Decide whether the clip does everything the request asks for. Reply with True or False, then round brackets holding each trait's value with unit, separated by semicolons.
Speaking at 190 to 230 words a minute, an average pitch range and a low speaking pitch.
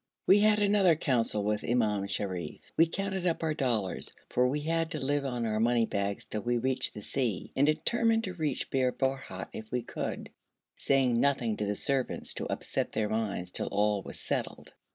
False (195 wpm; 6.4 semitones; 125 Hz)